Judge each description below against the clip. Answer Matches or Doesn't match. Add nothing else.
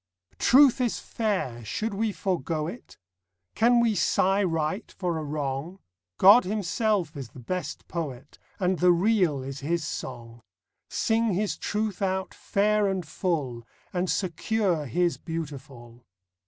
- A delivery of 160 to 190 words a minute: Doesn't match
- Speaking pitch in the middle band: Matches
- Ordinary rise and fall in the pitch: Doesn't match